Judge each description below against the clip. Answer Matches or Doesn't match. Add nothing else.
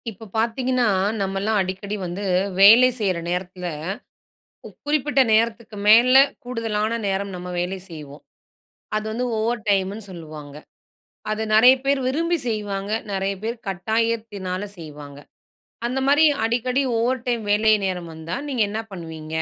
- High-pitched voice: Matches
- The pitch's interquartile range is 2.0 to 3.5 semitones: Doesn't match